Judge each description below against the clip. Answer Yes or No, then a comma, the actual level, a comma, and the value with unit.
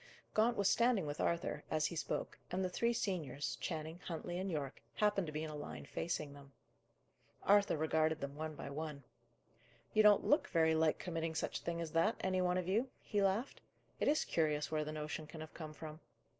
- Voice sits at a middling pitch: Yes, medium, 160 Hz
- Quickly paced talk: Yes, fast, 210 wpm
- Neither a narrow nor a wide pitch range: Yes, average, 3.8 semitones